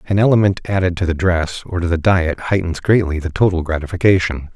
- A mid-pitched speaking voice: No, very low, 90 Hz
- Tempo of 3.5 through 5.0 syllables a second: No, 5.9 syllables/s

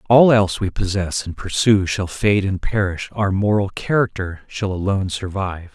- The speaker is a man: Yes, male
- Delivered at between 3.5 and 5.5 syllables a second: Yes, 4.9 syllables/s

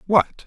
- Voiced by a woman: No, male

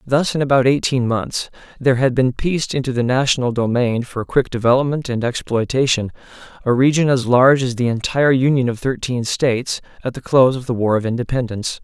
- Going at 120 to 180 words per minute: No, average, 190 wpm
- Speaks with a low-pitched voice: Yes, low, 125 Hz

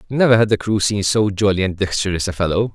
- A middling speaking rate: No, fast, 240 wpm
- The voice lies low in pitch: Yes, low, 100 Hz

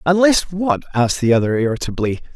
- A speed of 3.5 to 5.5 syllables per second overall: No, 6.0 syllables/s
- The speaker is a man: Yes, male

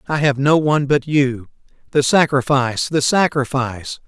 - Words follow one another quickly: No, average, 145 wpm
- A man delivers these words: Yes, male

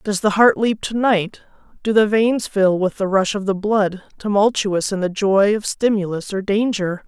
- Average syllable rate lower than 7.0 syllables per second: Yes, 4.5 syllables/s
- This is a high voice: Yes, high, 205 Hz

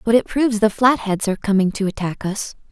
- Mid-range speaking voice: No, high, 210 Hz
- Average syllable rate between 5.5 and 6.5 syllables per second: Yes, 6.1 syllables/s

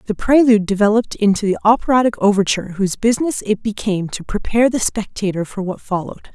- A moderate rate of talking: Yes, average, 170 wpm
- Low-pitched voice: No, high, 210 Hz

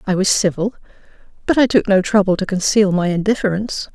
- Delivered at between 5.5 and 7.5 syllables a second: Yes, 6.2 syllables/s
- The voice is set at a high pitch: Yes, high, 200 Hz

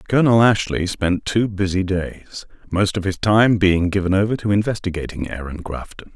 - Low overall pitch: Yes, very low, 95 Hz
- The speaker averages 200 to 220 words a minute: No, average, 165 wpm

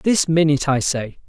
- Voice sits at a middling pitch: Yes, medium, 150 Hz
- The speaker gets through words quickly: No, average, 190 wpm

